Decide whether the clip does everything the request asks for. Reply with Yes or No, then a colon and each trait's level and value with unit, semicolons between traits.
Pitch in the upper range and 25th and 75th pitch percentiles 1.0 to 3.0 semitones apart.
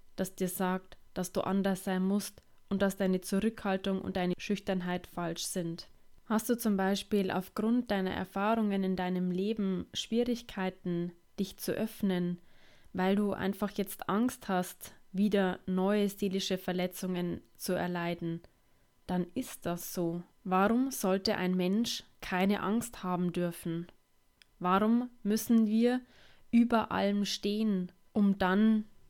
Yes: high, 195 Hz; narrow, 2.5 semitones